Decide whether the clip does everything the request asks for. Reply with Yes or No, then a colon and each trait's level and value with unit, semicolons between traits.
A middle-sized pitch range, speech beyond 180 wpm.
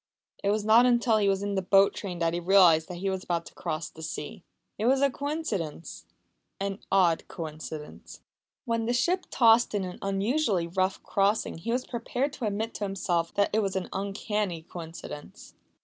Yes: average, 4.4 semitones; average, 190 wpm